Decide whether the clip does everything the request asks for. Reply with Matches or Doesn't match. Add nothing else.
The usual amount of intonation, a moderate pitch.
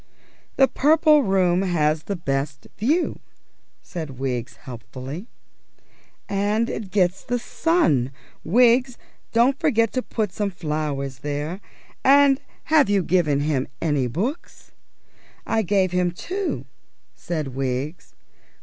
Doesn't match